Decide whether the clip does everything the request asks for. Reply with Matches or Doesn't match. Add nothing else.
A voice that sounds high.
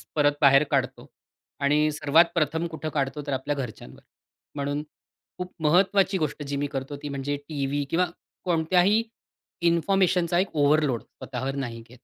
Doesn't match